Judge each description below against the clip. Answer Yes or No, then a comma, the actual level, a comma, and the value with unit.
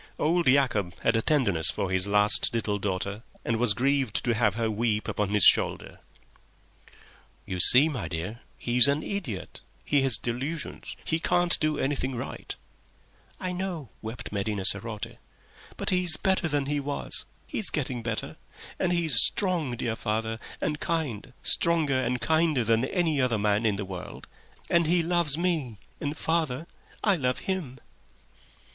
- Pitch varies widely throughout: Yes, wide, 6.5 semitones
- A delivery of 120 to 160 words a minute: Yes, average, 150 wpm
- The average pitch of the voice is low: Yes, low, 125 Hz